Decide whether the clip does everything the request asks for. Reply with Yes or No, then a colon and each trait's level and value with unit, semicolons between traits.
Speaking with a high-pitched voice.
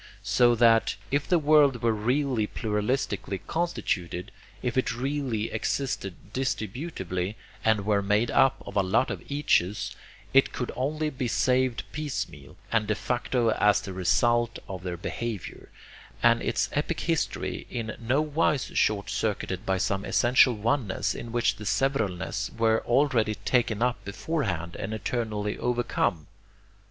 No: low, 115 Hz